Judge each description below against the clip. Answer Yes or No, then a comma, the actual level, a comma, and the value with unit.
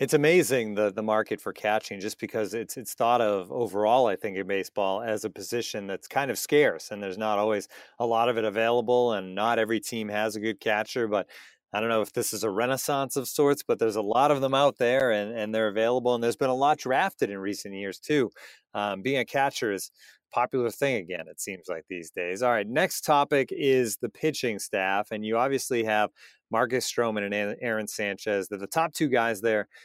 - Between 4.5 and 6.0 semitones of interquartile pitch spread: No, average, 3.5 semitones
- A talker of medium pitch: No, low, 115 Hz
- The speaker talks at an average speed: No, fast, 225 wpm